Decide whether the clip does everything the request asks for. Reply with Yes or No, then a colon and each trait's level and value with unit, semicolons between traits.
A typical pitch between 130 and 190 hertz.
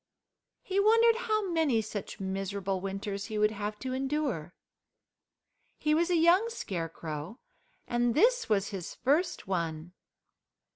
No: high, 220 Hz